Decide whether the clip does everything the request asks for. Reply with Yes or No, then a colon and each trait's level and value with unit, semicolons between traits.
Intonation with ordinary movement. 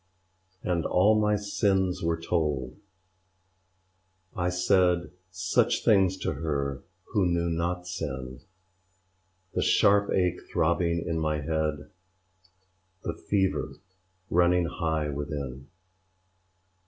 Yes: average, 3.2 semitones